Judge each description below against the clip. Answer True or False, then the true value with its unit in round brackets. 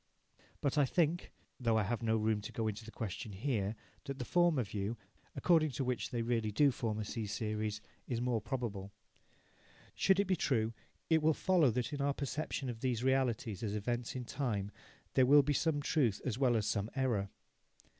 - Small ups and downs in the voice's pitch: False (4.4 semitones)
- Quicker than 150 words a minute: True (200 wpm)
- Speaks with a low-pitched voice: True (120 Hz)